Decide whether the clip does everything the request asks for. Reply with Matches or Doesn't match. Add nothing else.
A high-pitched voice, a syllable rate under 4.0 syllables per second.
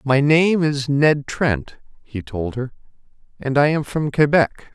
Doesn't match